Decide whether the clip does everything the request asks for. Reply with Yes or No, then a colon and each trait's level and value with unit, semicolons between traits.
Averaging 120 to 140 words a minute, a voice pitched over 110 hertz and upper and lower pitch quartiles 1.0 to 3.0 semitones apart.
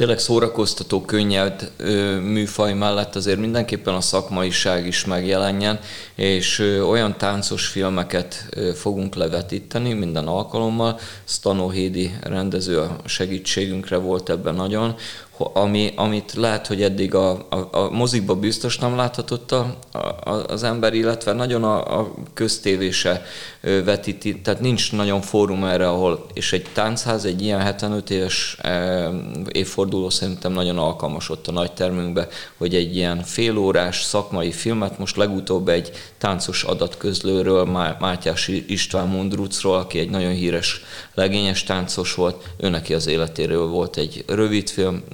No: average, 130 wpm; very low, 95 Hz; narrow, 2.4 semitones